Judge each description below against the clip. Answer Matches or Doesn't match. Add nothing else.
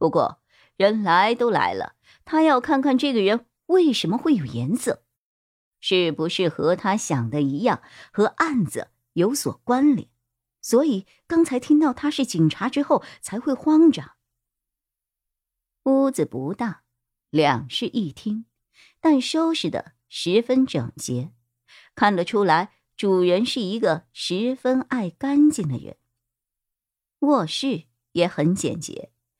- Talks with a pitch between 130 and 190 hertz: Doesn't match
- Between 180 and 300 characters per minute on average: Matches